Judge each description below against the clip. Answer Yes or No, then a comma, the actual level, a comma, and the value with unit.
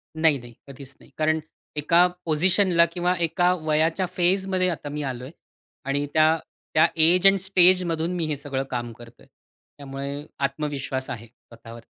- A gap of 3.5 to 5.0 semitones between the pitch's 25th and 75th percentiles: Yes, average, 4.3 semitones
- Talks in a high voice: No, medium, 155 Hz